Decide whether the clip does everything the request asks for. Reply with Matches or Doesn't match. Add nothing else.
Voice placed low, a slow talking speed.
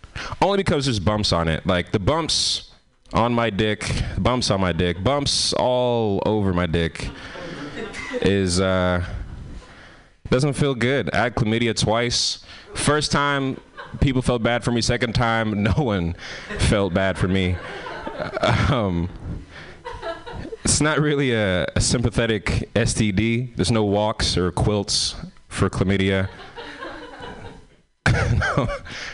Matches